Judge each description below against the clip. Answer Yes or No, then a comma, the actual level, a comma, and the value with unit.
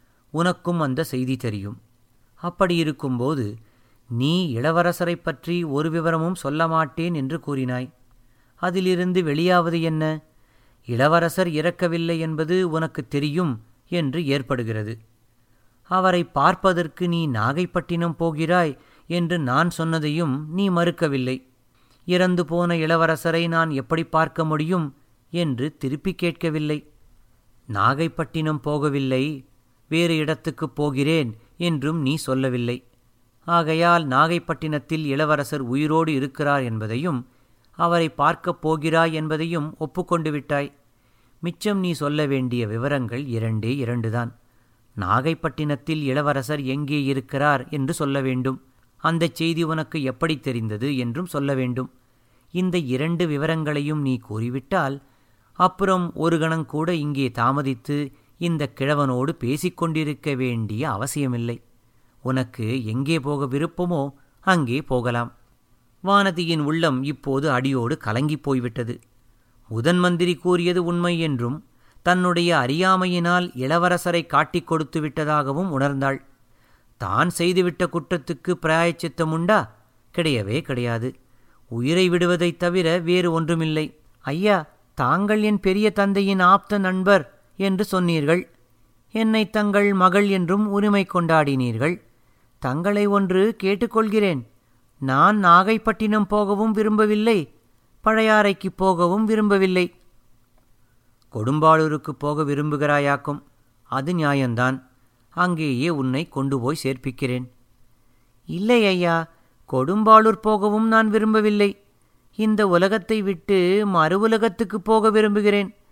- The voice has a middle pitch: Yes, medium, 155 Hz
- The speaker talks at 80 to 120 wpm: Yes, average, 95 wpm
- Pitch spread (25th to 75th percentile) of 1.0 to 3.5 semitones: No, wide, 5.4 semitones